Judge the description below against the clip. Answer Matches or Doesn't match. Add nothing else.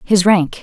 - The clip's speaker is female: Matches